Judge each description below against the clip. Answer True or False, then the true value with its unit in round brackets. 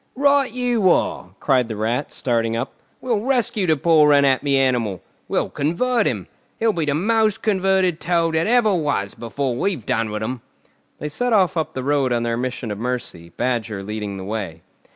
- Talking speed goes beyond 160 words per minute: True (185 wpm)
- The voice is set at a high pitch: False (140 Hz)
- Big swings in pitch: True (8.7 semitones)